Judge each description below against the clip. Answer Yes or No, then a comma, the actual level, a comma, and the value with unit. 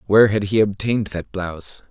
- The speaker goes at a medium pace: Yes, average, 190 wpm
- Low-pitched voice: Yes, low, 100 Hz